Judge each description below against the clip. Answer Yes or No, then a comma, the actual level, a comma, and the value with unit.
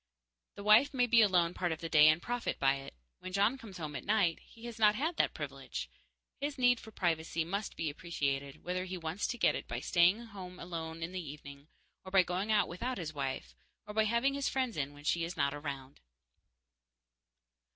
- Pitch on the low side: No, medium, 180 Hz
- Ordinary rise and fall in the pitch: No, wide, 5.8 semitones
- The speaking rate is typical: No, fast, 215 wpm